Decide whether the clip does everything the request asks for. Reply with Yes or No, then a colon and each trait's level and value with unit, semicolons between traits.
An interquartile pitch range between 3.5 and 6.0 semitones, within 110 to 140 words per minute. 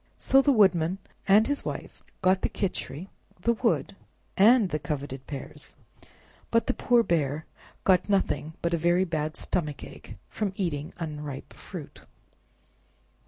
Yes: average, 5.2 semitones; slow, 135 wpm